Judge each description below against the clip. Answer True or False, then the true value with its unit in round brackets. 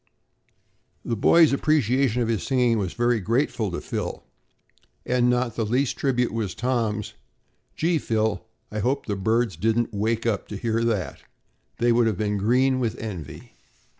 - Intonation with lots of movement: False (2.7 semitones)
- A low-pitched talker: True (115 Hz)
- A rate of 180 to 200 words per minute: False (160 wpm)